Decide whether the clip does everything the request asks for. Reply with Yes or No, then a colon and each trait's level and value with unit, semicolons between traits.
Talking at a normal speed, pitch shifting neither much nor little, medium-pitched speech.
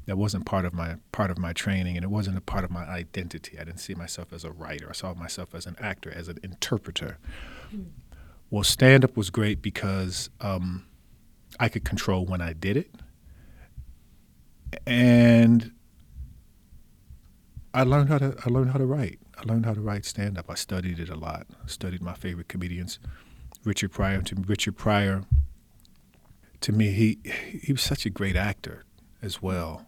No: average, 175 wpm; average, 4.2 semitones; very low, 95 Hz